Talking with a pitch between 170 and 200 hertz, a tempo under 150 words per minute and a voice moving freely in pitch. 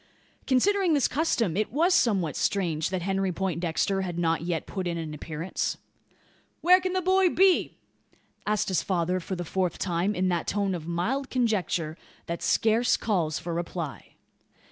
No: medium, 185 Hz; average, 165 wpm; wide, 5.9 semitones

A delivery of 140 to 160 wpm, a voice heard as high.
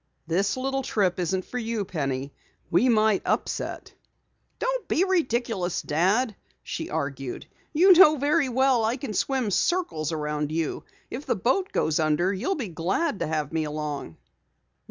Yes: average, 155 wpm; high, 200 Hz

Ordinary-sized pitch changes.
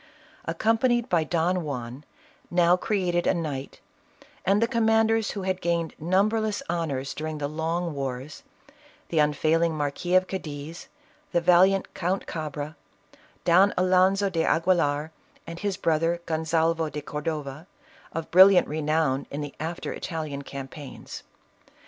Yes: average, 3.6 semitones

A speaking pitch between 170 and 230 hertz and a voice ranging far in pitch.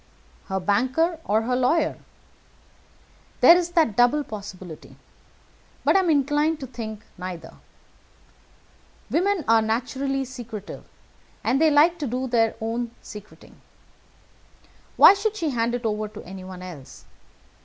No: high, 245 Hz; wide, 5.9 semitones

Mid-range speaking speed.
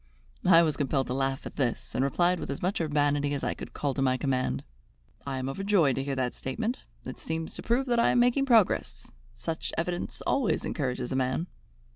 No: fast, 210 wpm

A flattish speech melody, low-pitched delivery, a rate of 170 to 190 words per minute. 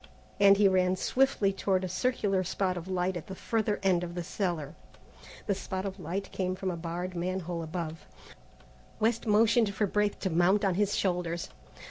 No: narrow, 2.3 semitones; medium, 185 Hz; average, 180 wpm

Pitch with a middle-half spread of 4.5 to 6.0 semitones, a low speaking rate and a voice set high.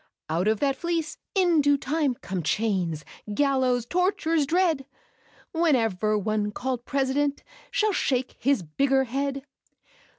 Yes: wide, 5.4 semitones; slow, 125 wpm; very high, 270 Hz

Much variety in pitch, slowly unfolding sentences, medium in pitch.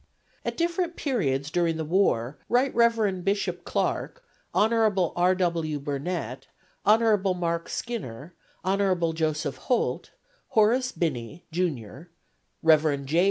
Yes: wide, 5.7 semitones; slow, 115 wpm; medium, 175 Hz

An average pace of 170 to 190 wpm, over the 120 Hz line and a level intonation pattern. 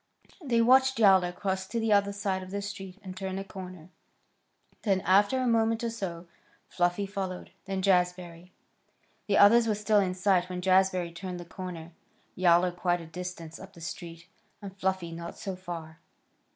Yes: average, 175 wpm; medium, 185 Hz; narrow, 2.3 semitones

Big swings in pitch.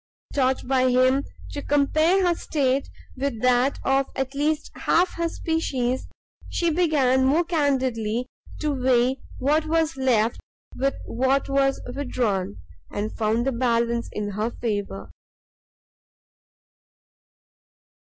No: average, 3.2 semitones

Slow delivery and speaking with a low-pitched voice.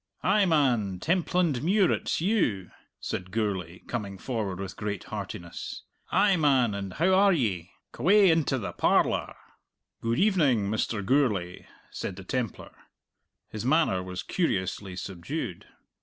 Yes: slow, 125 wpm; low, 115 Hz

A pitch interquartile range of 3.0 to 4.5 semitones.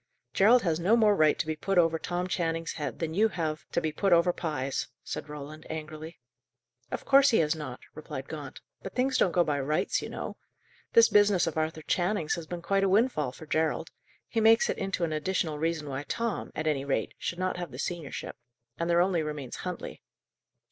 Yes: average, 3.6 semitones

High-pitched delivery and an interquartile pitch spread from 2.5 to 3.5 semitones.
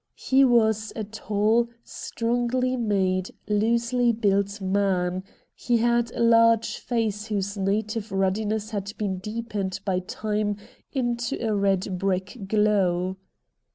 Yes: high, 210 Hz; average, 3.0 semitones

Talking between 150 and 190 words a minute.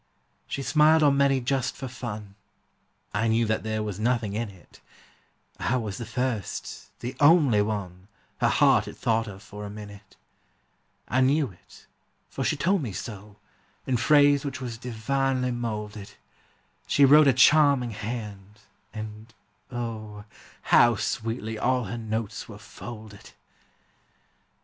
No: average, 140 wpm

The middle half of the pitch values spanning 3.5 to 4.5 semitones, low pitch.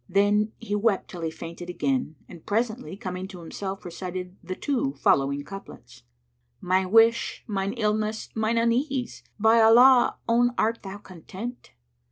No: average, 3.9 semitones; high, 205 Hz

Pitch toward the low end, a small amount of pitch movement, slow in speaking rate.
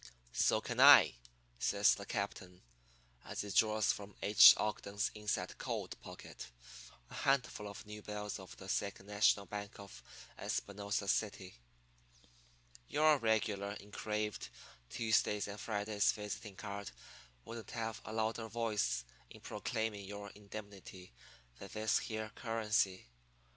Yes: low, 105 Hz; narrow, 1.4 semitones; slow, 125 wpm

